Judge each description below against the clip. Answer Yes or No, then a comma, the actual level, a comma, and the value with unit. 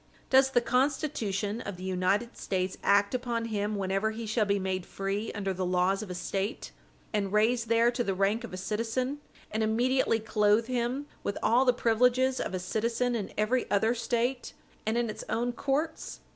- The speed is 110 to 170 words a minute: No, average, 185 wpm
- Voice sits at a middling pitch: No, high, 225 Hz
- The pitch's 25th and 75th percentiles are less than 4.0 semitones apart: Yes, average, 3.4 semitones